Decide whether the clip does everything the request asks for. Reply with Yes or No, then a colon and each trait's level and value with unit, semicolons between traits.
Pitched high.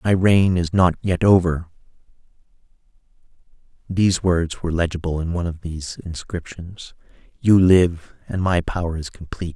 No: very low, 90 Hz